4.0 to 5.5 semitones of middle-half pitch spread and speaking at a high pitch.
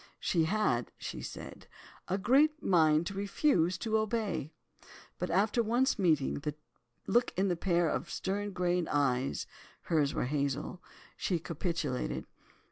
No: average, 5.2 semitones; medium, 180 Hz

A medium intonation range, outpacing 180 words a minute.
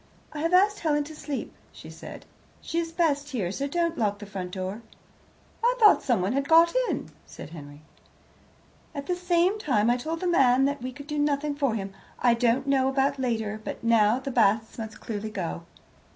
No: wide, 5.7 semitones; average, 195 wpm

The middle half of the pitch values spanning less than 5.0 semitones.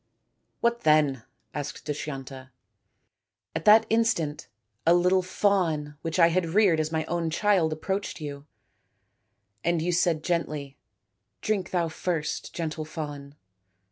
Yes: average, 3.4 semitones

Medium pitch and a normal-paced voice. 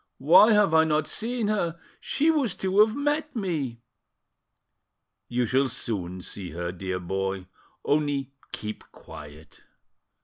No: medium, 145 Hz; slow, 130 wpm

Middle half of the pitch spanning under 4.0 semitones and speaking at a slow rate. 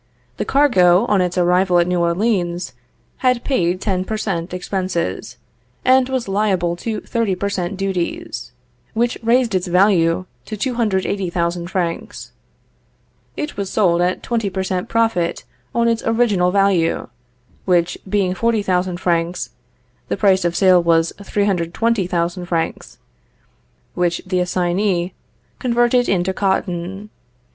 Yes: average, 3.3 semitones; slow, 125 wpm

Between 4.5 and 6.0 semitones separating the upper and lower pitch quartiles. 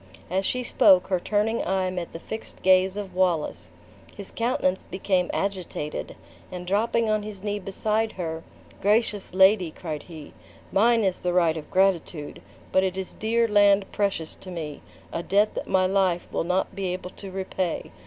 No: narrow, 2.4 semitones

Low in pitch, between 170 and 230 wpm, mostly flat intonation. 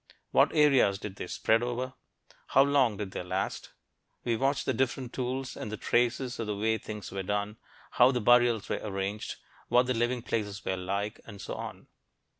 No: low, 115 Hz; average, 190 wpm; average, 3.7 semitones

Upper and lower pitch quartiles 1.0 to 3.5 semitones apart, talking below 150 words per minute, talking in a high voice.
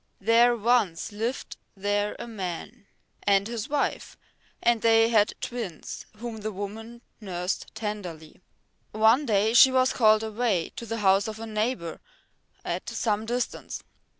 Yes: narrow, 2.5 semitones; average, 140 wpm; high, 220 Hz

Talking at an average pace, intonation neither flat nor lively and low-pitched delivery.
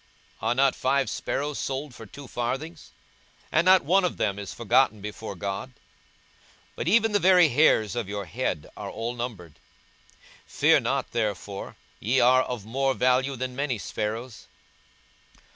Yes: average, 160 wpm; average, 4.4 semitones; low, 125 Hz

